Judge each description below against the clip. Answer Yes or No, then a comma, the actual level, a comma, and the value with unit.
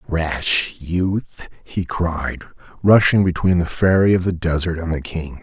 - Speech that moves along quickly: No, average, 155 wpm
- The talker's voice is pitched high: No, very low, 85 Hz